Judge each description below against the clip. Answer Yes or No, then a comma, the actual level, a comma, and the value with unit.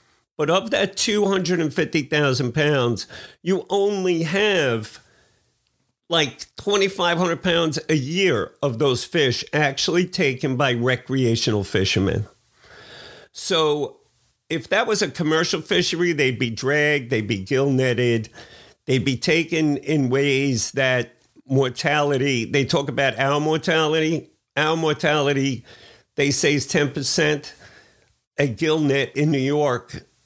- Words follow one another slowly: Yes, slow, 115 wpm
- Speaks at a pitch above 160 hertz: No, medium, 145 Hz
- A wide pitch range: No, average, 3.9 semitones